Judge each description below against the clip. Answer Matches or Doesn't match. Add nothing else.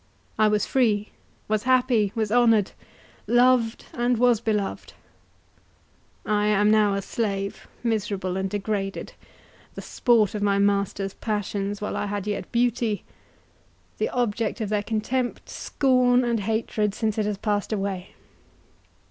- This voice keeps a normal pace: Doesn't match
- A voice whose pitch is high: Matches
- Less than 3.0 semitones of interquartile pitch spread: Matches